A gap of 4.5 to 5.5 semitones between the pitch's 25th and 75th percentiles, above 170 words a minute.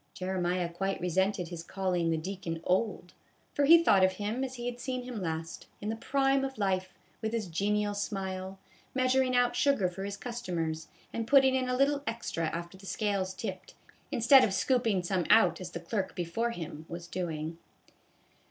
Yes: average, 5.1 semitones; average, 180 wpm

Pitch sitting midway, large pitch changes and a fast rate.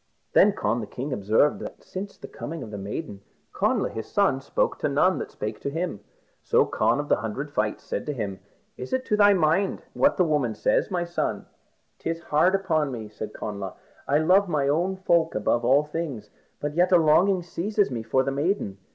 Yes: medium, 150 Hz; wide, 7.1 semitones; fast, 210 wpm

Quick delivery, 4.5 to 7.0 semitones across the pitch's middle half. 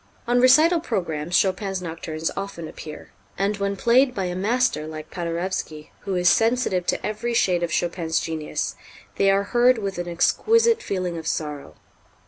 No: average, 160 wpm; wide, 5.4 semitones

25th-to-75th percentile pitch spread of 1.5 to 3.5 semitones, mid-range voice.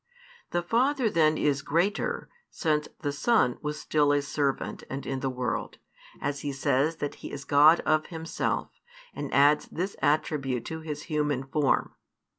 Yes: narrow, 2.4 semitones; medium, 150 Hz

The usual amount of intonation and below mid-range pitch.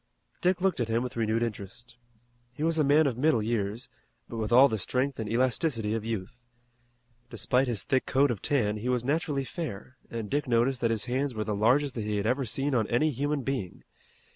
Yes: average, 3.8 semitones; low, 125 Hz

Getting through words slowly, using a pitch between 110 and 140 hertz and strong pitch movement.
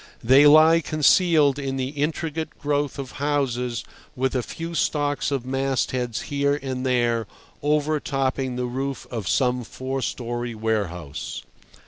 No: slow, 130 wpm; low, 135 Hz; average, 2.7 semitones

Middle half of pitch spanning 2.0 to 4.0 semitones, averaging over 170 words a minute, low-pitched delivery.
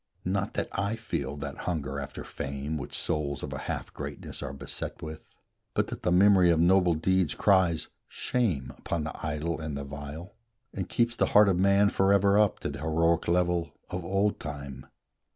No: average, 4.5 semitones; average, 185 wpm; very low, 85 Hz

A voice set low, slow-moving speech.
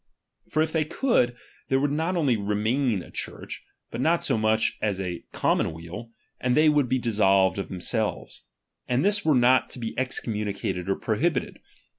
No: low, 120 Hz; average, 175 wpm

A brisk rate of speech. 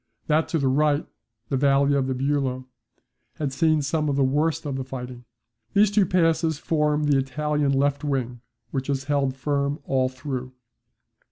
No: average, 165 wpm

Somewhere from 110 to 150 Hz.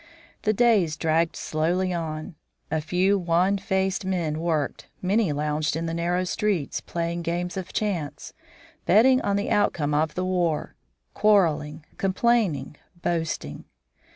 No: medium, 175 Hz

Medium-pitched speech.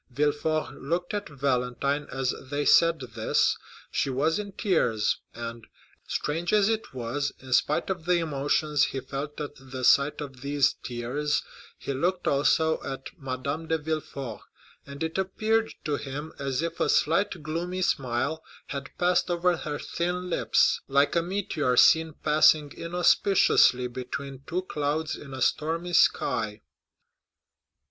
Yes: medium, 150 Hz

